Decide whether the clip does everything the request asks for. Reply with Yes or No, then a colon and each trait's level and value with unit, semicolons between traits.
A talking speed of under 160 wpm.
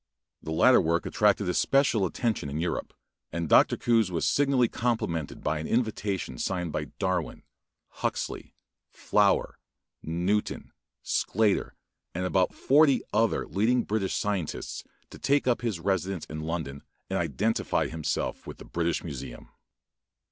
Yes: slow, 135 wpm